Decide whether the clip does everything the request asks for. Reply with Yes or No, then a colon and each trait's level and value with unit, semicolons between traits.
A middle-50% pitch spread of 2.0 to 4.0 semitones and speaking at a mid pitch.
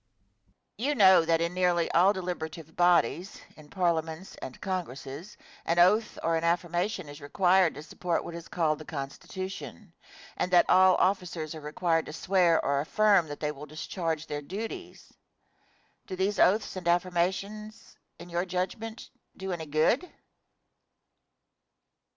Yes: average, 2.8 semitones; medium, 175 Hz